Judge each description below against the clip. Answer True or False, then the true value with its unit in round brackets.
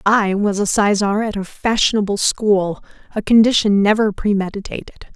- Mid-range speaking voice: False (205 Hz)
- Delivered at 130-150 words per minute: True (140 wpm)